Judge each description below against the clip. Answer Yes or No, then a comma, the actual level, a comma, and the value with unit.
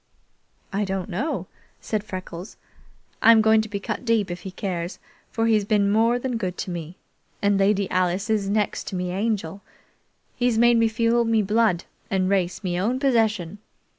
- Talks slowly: No, average, 180 wpm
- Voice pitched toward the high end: Yes, high, 205 Hz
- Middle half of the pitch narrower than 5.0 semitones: Yes, average, 3.3 semitones